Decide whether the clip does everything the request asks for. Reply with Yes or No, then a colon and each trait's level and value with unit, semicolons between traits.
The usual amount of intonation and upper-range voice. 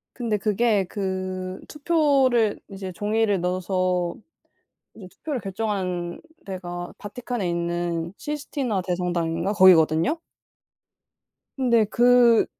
Yes: average, 4.7 semitones; high, 195 Hz